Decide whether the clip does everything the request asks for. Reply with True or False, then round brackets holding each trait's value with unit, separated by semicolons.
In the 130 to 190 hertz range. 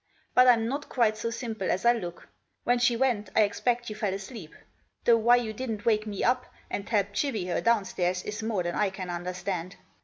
False (215 Hz)